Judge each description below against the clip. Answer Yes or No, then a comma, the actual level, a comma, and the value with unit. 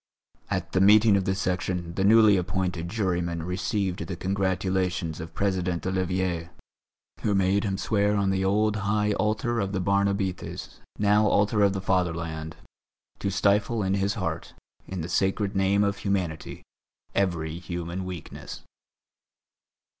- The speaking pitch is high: No, very low, 95 Hz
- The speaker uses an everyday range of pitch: No, narrow, 2.1 semitones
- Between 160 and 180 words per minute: No, average, 145 wpm